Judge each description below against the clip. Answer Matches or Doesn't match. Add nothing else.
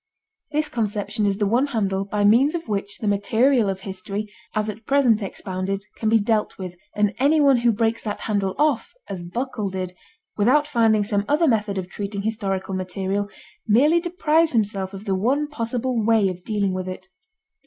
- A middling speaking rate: Matches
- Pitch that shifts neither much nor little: Matches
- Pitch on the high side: Matches